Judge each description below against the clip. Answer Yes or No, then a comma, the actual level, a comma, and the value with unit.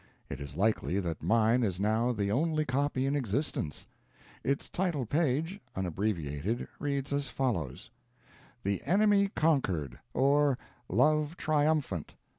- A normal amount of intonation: No, wide, 7.0 semitones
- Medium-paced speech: No, slow, 120 wpm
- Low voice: Yes, low, 130 Hz